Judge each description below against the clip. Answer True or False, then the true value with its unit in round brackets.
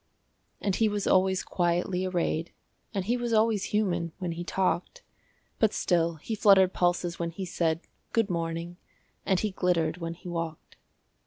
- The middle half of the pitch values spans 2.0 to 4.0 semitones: True (2.6 semitones)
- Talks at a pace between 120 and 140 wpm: False (160 wpm)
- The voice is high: False (180 Hz)